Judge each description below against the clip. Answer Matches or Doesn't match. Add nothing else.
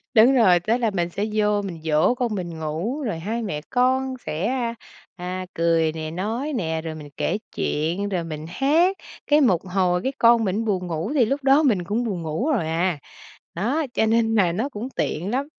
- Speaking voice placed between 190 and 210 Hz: Matches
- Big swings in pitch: Matches